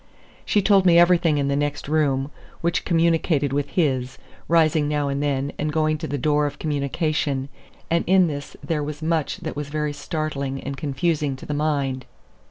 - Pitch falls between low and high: Yes, medium, 150 Hz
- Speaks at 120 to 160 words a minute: No, average, 180 wpm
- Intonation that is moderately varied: No, narrow, 2.3 semitones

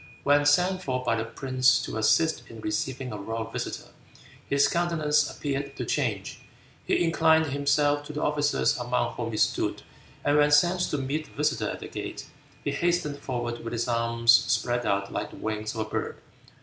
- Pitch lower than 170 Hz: Yes, low, 135 Hz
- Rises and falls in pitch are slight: No, average, 4.2 semitones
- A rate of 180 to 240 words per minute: Yes, average, 190 wpm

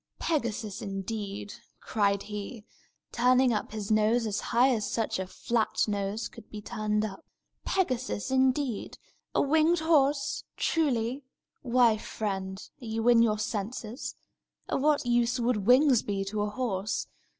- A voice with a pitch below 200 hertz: No, high, 225 Hz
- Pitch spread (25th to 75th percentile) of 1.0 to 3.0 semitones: No, average, 3.5 semitones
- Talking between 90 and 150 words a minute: Yes, average, 140 wpm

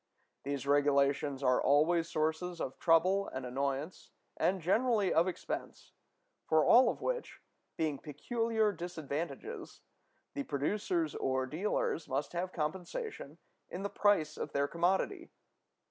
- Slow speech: Yes, slow, 125 wpm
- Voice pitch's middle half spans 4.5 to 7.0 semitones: Yes, wide, 5.4 semitones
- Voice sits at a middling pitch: Yes, medium, 165 Hz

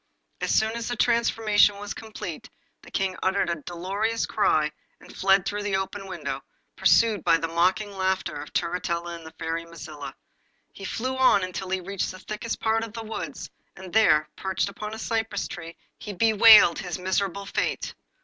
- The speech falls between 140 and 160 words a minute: No, average, 180 wpm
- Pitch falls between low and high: No, high, 195 Hz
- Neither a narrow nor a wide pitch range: Yes, average, 3.9 semitones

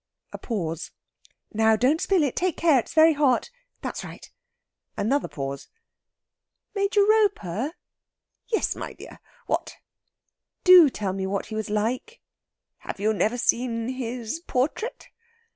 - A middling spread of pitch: No, wide, 7.1 semitones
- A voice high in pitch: Yes, very high, 250 Hz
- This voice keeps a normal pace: No, slow, 130 wpm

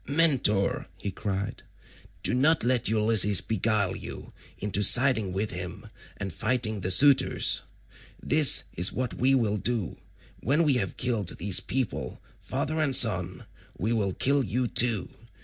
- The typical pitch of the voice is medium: No, low, 110 Hz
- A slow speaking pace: No, average, 145 wpm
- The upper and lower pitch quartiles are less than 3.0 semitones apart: No, average, 4.8 semitones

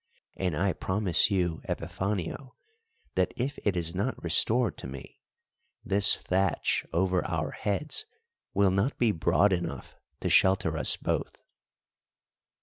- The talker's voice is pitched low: Yes, very low, 95 Hz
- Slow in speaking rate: Yes, slow, 130 wpm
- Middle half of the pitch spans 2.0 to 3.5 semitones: Yes, average, 2.9 semitones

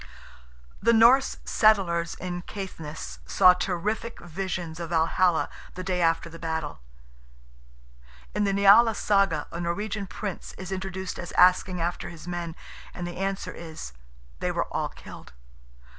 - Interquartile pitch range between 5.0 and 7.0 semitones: No, average, 2.7 semitones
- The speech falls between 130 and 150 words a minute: Yes, average, 140 wpm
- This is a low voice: No, medium, 180 Hz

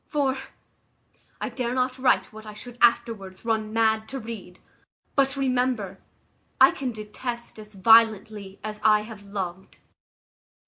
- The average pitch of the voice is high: Yes, high, 220 Hz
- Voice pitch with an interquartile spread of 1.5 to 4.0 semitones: Yes, average, 2.9 semitones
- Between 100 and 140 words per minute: Yes, slow, 135 wpm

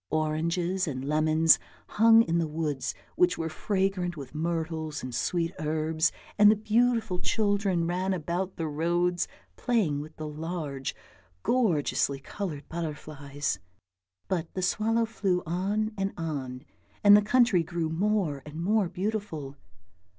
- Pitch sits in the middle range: Yes, medium, 170 Hz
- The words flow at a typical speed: No, slow, 130 wpm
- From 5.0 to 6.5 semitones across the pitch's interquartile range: No, average, 4.4 semitones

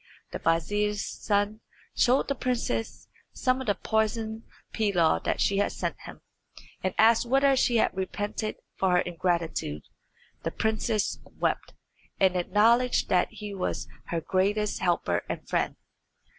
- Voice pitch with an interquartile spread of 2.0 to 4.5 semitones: Yes, average, 3.5 semitones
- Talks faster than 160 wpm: No, average, 140 wpm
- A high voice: Yes, high, 210 Hz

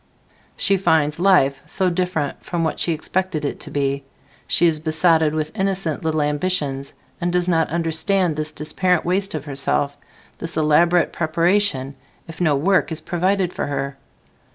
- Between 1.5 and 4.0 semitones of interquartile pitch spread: Yes, average, 3.2 semitones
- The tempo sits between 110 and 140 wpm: No, average, 155 wpm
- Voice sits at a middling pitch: Yes, medium, 160 Hz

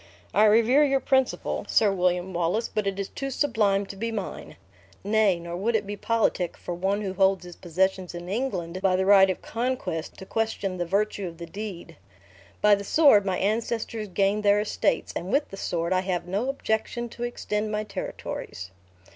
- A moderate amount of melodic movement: Yes, average, 3.1 semitones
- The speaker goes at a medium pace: Yes, average, 190 wpm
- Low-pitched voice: No, high, 200 Hz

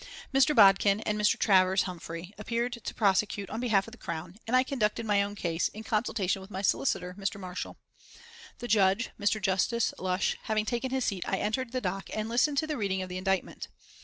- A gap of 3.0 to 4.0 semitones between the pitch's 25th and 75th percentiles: Yes, average, 3.5 semitones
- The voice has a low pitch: No, high, 205 Hz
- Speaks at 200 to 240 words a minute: Yes, fast, 205 wpm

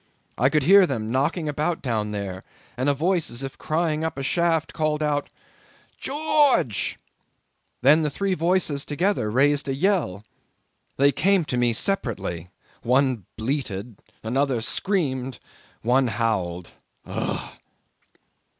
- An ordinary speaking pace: No, slow, 125 wpm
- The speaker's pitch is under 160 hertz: Yes, medium, 140 Hz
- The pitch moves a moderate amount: No, wide, 5.7 semitones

